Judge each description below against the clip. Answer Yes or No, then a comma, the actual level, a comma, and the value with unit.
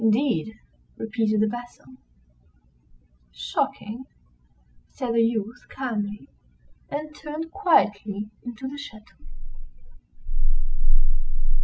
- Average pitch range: Yes, average, 3.9 semitones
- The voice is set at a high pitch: Yes, high, 230 Hz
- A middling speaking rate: No, slow, 75 wpm